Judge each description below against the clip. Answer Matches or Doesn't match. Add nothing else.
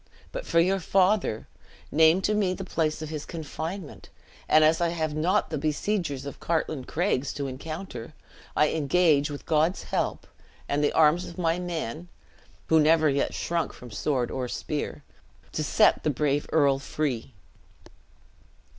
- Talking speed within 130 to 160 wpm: Matches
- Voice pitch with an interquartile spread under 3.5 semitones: Matches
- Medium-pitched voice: Matches